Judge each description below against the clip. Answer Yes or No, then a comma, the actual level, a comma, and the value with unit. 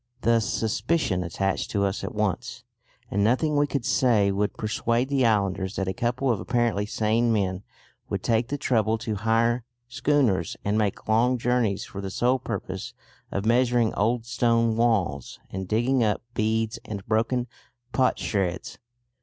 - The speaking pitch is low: Yes, low, 115 Hz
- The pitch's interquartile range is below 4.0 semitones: Yes, average, 3.2 semitones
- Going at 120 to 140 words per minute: No, average, 155 wpm